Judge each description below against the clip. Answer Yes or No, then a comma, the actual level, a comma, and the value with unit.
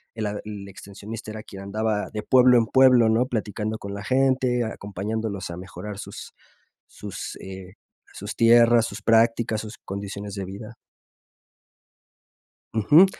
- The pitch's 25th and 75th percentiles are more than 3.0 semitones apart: No, narrow, 2.6 semitones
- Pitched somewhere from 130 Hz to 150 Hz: No, low, 110 Hz